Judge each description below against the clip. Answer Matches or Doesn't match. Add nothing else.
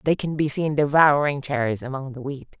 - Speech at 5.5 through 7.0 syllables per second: Doesn't match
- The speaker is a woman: Matches